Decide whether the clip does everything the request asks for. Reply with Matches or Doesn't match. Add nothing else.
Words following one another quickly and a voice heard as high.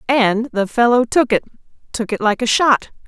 Doesn't match